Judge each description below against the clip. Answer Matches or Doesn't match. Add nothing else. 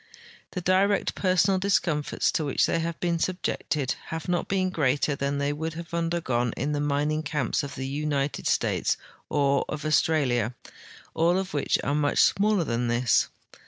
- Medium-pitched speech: Matches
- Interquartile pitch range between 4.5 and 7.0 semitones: Doesn't match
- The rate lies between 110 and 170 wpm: Matches